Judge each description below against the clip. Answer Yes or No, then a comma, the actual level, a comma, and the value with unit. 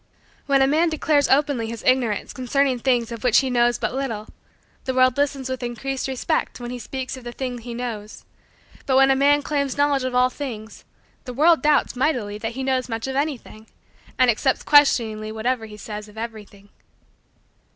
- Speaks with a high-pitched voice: Yes, very high, 255 Hz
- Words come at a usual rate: Yes, average, 190 wpm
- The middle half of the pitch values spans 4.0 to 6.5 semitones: No, average, 2.9 semitones